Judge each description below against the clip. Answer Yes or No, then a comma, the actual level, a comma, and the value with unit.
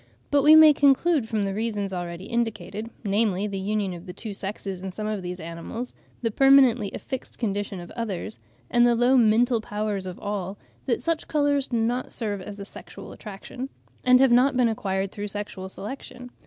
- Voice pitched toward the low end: No, high, 215 Hz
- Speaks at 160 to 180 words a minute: No, average, 190 wpm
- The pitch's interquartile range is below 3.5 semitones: No, average, 4.0 semitones